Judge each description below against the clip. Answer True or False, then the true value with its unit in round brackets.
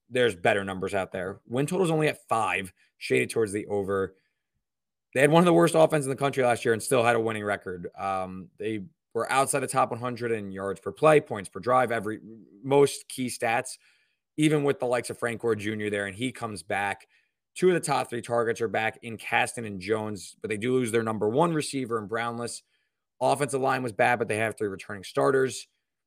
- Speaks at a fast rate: True (220 wpm)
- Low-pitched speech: True (115 Hz)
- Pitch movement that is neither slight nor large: True (4.2 semitones)